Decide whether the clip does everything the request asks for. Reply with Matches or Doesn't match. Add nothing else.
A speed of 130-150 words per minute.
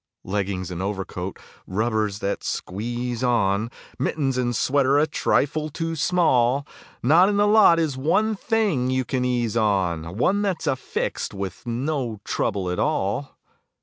Matches